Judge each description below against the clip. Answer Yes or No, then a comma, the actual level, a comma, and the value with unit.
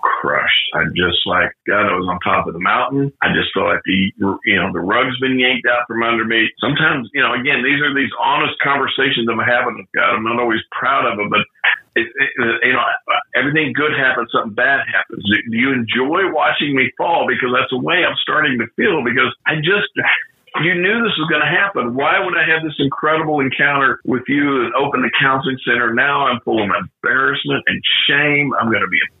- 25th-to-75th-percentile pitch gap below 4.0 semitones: No, average, 4.5 semitones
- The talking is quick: Yes, fast, 220 wpm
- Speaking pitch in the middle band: No, low, 130 Hz